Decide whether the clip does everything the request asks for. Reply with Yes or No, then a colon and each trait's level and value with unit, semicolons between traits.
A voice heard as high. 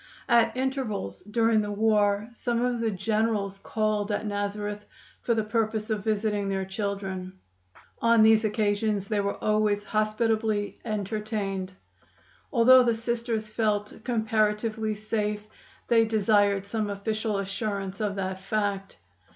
Yes: high, 215 Hz